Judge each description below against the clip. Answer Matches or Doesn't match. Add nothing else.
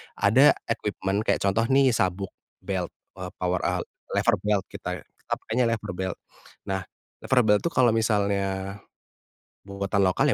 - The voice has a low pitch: Matches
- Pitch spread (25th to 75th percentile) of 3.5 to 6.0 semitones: Doesn't match